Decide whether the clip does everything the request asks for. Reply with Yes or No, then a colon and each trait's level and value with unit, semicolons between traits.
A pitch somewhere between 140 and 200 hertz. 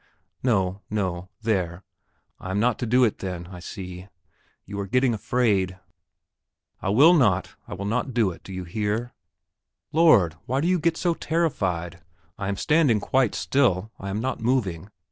No: low, 105 Hz